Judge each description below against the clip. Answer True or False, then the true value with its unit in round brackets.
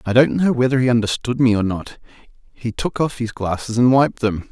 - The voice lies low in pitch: True (120 Hz)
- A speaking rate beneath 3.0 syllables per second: False (5.4 syllables/s)